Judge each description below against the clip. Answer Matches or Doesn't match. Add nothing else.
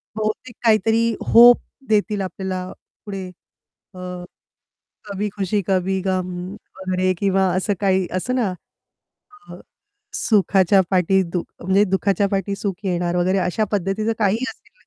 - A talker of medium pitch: Doesn't match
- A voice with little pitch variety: Matches